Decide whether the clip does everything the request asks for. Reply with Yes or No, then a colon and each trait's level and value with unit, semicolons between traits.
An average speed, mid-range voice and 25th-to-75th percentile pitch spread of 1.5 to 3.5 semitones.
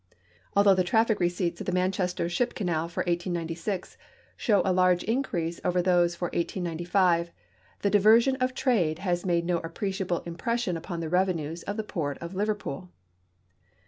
Yes: average, 155 wpm; medium, 180 Hz; average, 2.9 semitones